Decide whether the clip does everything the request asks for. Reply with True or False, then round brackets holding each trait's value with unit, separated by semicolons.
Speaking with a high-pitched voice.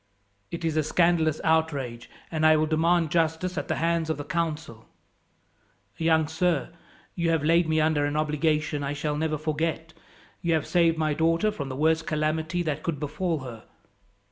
False (160 Hz)